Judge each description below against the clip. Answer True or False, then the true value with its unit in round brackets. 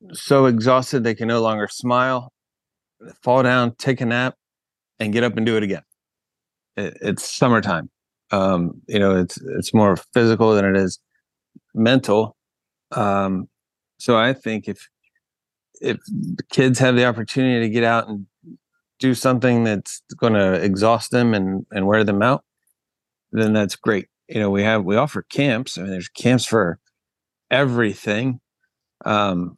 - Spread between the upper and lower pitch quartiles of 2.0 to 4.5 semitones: True (3.7 semitones)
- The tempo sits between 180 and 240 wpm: False (155 wpm)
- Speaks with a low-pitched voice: True (115 Hz)